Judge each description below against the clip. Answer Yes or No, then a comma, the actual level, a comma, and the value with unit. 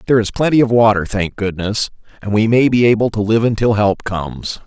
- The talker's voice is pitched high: No, low, 110 Hz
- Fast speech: Yes, fast, 220 wpm